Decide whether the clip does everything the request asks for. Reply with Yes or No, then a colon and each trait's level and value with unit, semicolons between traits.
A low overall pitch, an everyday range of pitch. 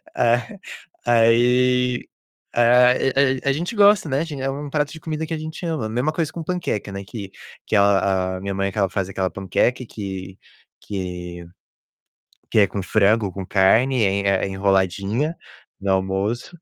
No: low, 115 Hz; wide, 5.7 semitones